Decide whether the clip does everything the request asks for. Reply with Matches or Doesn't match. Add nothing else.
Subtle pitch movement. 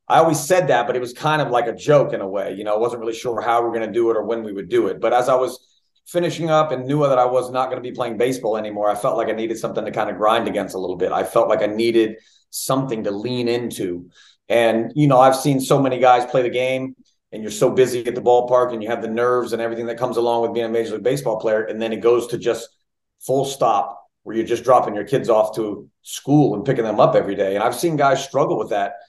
Matches